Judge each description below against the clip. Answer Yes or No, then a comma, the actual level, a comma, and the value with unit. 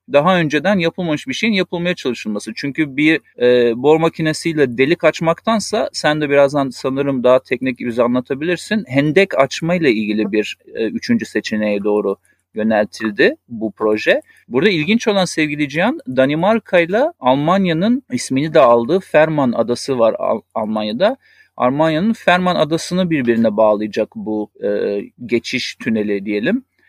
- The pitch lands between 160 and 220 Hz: No, medium, 145 Hz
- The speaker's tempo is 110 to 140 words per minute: Yes, average, 135 wpm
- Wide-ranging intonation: Yes, wide, 7.0 semitones